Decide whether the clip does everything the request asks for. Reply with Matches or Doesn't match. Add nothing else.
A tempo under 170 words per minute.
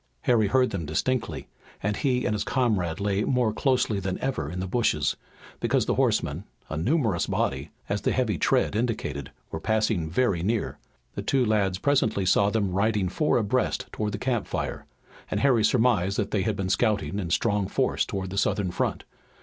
Doesn't match